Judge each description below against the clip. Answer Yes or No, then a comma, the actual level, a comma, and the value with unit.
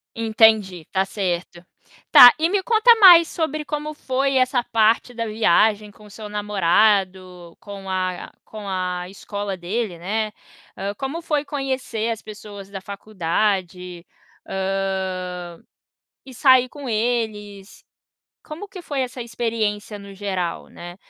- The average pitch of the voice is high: Yes, high, 210 Hz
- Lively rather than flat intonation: No, average, 4.5 semitones